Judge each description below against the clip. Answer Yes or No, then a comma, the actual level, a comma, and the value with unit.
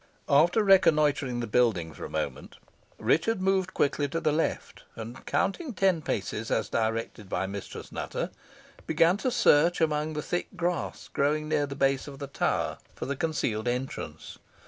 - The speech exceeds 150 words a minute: Yes, average, 165 wpm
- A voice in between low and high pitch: Yes, medium, 150 Hz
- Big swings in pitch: Yes, wide, 5.9 semitones